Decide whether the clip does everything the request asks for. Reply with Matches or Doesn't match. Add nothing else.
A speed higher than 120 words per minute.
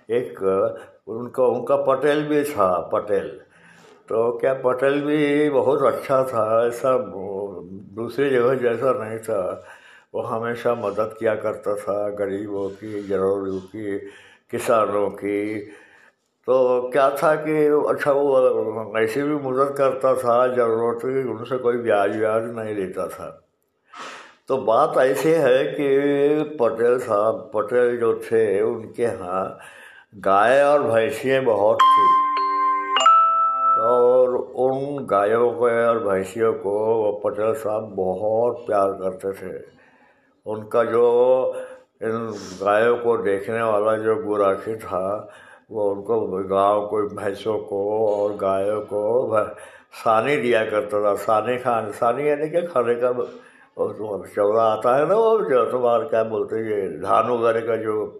Matches